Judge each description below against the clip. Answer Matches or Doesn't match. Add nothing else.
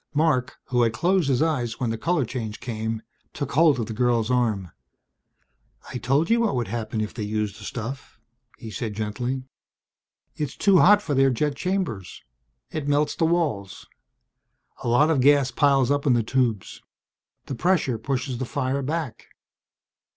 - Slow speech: Doesn't match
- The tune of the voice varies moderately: Matches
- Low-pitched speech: Matches